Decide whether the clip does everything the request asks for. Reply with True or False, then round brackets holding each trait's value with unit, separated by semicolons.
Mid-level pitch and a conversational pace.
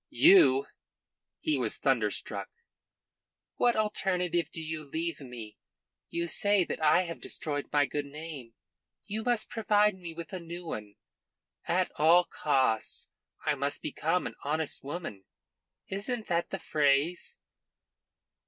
False (165 Hz; 130 wpm)